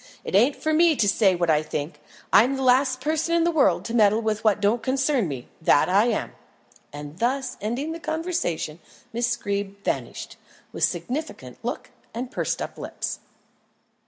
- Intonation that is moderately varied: No, wide, 5.8 semitones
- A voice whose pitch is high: Yes, high, 235 Hz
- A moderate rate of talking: Yes, average, 180 wpm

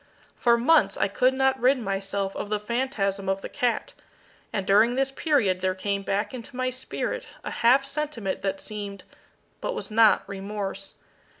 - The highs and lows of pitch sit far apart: No, average, 4.7 semitones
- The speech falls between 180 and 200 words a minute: No, average, 170 wpm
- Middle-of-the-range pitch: No, high, 215 Hz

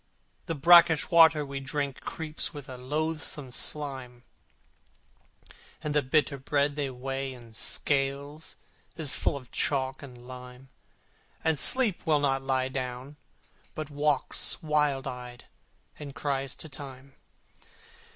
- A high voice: No, medium, 140 Hz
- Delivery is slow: Yes, slow, 130 wpm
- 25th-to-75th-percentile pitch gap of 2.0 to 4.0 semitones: Yes, narrow, 2.4 semitones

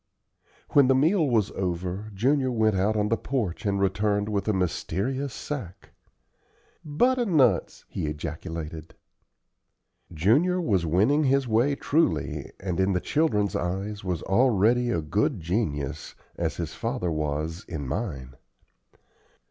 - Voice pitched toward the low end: Yes, low, 100 Hz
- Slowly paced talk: Yes, slow, 130 wpm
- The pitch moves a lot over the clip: Yes, wide, 7.2 semitones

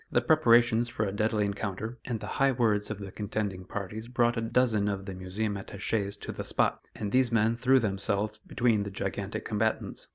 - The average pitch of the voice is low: Yes, low, 105 Hz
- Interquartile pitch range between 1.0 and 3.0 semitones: Yes, narrow, 2.6 semitones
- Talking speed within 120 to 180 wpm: No, average, 195 wpm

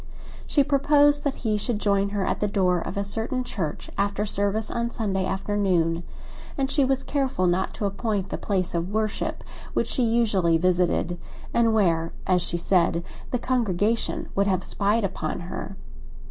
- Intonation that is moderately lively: Yes, average, 4.1 semitones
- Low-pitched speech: No, high, 200 Hz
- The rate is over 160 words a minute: Yes, average, 170 wpm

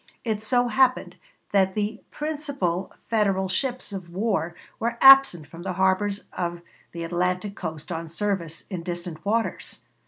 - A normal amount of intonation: Yes, average, 4.3 semitones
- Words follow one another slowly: No, average, 145 wpm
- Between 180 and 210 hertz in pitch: Yes, high, 190 Hz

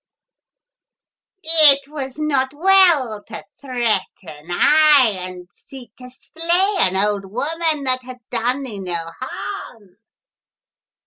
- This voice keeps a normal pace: No, slow, 115 wpm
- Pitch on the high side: Yes, very high, 255 Hz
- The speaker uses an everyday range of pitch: No, wide, 6.7 semitones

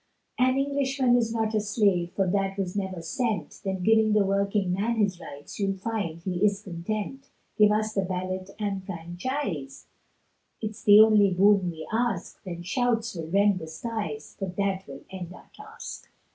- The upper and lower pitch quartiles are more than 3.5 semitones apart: No, average, 3.2 semitones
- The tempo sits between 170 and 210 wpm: Yes, average, 175 wpm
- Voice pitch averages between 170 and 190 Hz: No, high, 200 Hz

